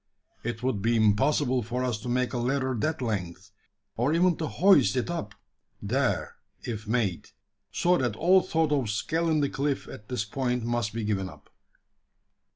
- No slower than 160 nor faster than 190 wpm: Yes, average, 170 wpm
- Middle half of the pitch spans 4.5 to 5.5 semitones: Yes, average, 5.1 semitones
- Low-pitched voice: Yes, low, 125 Hz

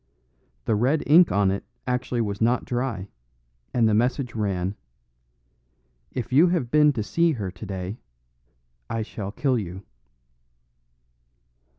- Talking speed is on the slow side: Yes, slow, 125 wpm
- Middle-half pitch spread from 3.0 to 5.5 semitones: Yes, average, 4.6 semitones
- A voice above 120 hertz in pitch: No, low, 115 Hz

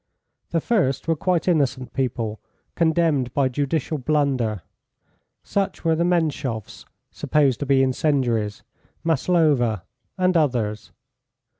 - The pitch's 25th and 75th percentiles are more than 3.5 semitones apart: Yes, average, 4.8 semitones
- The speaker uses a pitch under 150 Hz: Yes, medium, 140 Hz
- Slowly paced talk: Yes, slow, 110 wpm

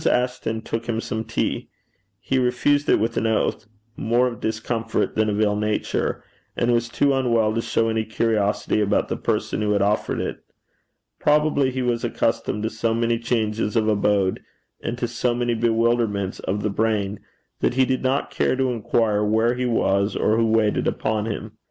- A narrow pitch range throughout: Yes, narrow, 2.1 semitones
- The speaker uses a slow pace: No, average, 180 wpm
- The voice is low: Yes, low, 115 Hz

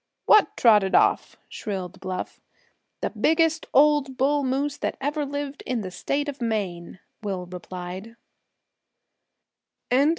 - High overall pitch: Yes, very high, 250 Hz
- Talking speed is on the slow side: Yes, slow, 120 wpm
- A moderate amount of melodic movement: No, wide, 7.4 semitones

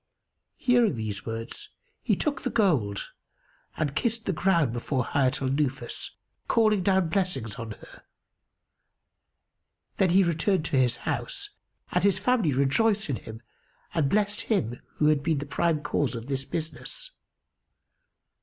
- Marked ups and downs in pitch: Yes, wide, 7.0 semitones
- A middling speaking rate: Yes, average, 145 wpm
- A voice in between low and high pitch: Yes, medium, 155 Hz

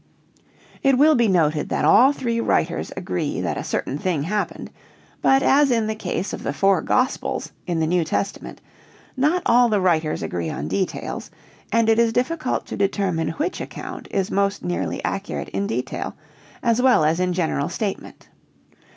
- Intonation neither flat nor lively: No, wide, 7.1 semitones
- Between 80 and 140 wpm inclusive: No, average, 175 wpm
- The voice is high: Yes, high, 200 Hz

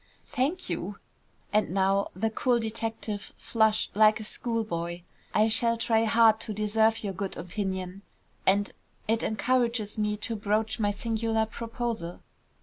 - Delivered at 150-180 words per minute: No, average, 140 wpm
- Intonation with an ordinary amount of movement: No, narrow, 1.9 semitones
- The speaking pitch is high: Yes, high, 220 Hz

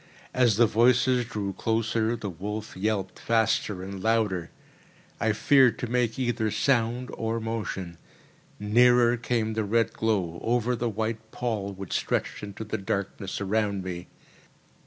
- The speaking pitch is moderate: No, low, 110 Hz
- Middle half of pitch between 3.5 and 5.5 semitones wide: No, average, 2.8 semitones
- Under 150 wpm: Yes, average, 140 wpm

